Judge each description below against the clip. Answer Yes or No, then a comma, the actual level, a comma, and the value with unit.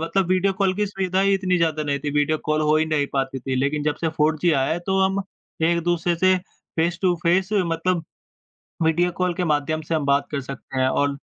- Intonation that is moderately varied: Yes, average, 3.9 semitones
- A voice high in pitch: No, medium, 160 Hz